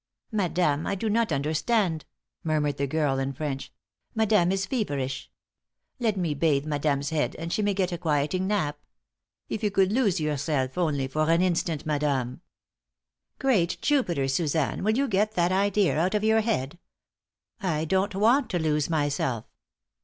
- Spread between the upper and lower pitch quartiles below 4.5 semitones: No, wide, 5.6 semitones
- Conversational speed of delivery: Yes, average, 160 wpm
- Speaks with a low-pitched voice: No, medium, 165 Hz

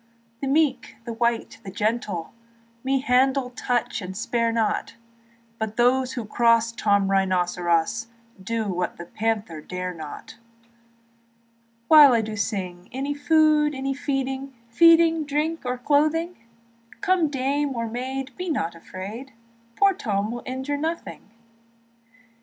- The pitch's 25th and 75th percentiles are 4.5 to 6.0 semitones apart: Yes, average, 5.2 semitones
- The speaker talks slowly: Yes, slow, 125 wpm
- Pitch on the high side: Yes, high, 245 Hz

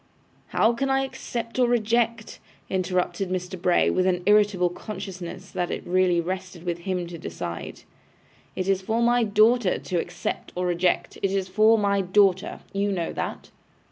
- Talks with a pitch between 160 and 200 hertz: Yes, high, 190 Hz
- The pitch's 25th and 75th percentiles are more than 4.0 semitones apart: No, average, 3.2 semitones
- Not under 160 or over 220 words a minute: Yes, average, 165 wpm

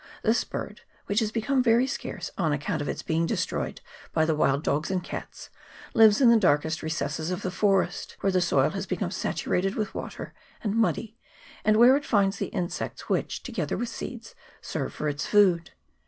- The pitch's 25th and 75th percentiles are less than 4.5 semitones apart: No, average, 5.3 semitones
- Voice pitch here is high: Yes, high, 195 Hz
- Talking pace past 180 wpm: Yes, average, 190 wpm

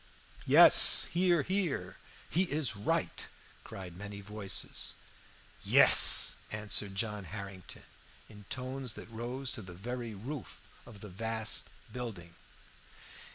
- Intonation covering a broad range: No, average, 4.3 semitones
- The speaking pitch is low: Yes, low, 110 Hz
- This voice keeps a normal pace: No, slow, 110 wpm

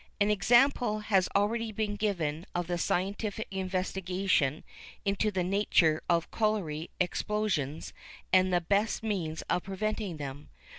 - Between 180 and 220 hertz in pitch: Yes, high, 190 Hz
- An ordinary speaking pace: No, slow, 130 wpm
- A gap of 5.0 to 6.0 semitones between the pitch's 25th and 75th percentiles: No, average, 3.6 semitones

